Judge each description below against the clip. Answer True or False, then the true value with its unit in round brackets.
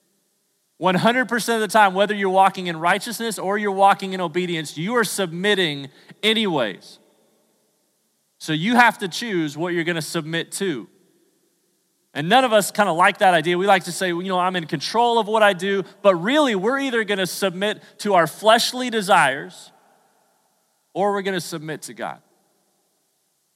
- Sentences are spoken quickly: False (175 wpm)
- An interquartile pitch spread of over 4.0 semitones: False (3.3 semitones)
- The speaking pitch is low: False (195 Hz)